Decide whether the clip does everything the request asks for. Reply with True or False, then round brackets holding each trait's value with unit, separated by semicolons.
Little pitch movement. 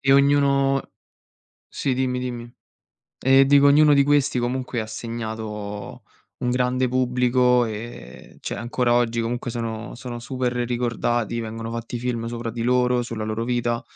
True (1.7 semitones)